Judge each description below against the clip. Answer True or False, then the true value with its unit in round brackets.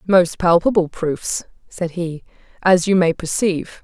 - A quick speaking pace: False (140 wpm)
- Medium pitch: True (175 Hz)